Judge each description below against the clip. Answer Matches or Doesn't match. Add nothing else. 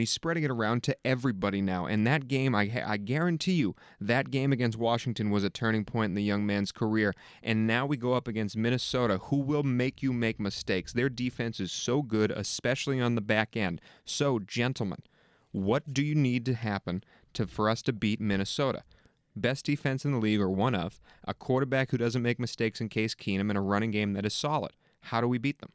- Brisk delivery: Matches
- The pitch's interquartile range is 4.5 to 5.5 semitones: Doesn't match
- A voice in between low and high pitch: Doesn't match